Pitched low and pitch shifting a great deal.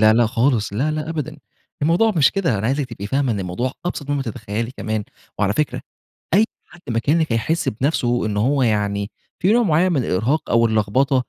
Yes: low, 130 Hz; wide, 6.0 semitones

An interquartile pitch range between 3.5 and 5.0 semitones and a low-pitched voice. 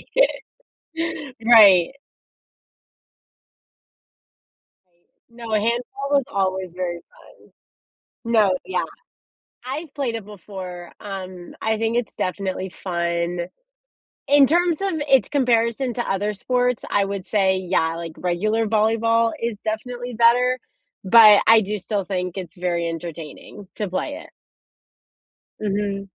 No: average, 4.1 semitones; high, 210 Hz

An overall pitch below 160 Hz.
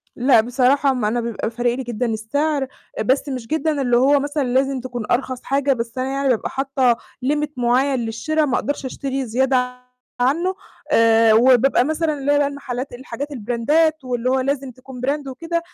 No: very high, 260 Hz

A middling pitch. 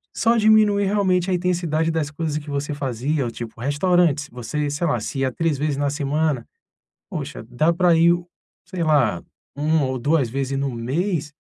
Yes: medium, 150 Hz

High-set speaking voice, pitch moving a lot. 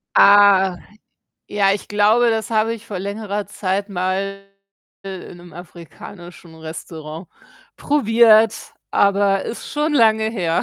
No: high, 200 Hz; average, 3.1 semitones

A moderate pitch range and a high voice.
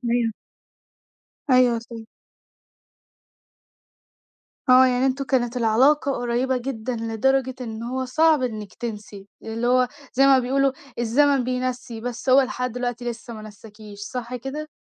No: narrow, 2.3 semitones; high, 245 Hz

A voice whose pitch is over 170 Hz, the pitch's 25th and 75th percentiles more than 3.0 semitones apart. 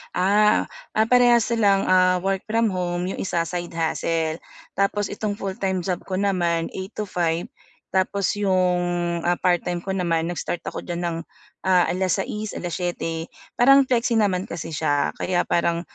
No: medium, 185 Hz; average, 2.7 semitones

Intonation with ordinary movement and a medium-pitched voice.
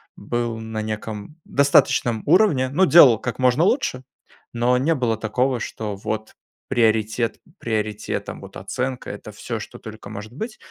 No: average, 3.1 semitones; low, 120 Hz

